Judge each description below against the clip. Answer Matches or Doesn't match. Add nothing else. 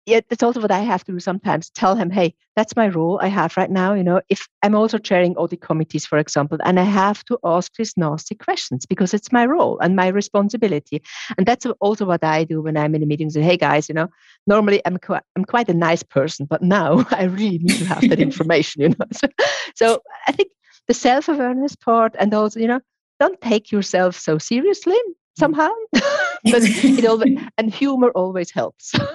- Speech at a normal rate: Doesn't match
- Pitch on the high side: Matches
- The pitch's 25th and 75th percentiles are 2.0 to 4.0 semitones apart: Doesn't match